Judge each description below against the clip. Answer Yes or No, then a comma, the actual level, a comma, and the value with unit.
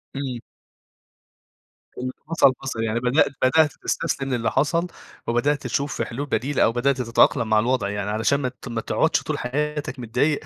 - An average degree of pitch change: Yes, average, 3.4 semitones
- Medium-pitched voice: No, low, 130 Hz